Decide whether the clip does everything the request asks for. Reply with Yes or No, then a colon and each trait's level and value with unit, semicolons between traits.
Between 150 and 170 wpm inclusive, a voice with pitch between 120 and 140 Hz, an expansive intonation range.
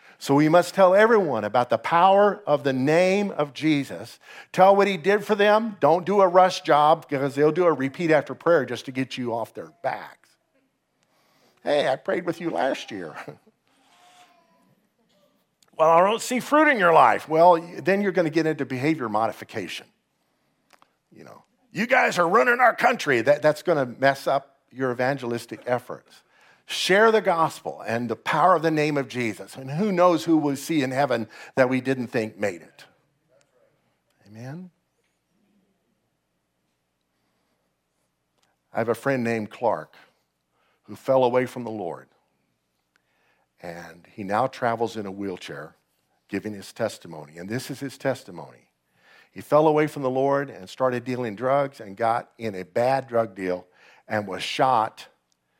Yes: average, 165 wpm; low, 135 Hz; wide, 6.8 semitones